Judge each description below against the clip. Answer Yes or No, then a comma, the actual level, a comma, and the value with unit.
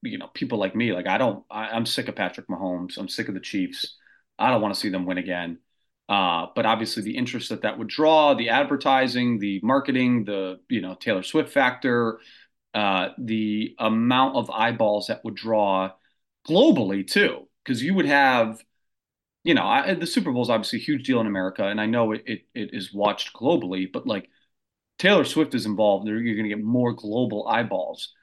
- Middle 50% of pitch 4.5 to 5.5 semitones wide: No, average, 3.7 semitones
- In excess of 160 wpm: Yes, average, 200 wpm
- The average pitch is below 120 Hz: Yes, low, 110 Hz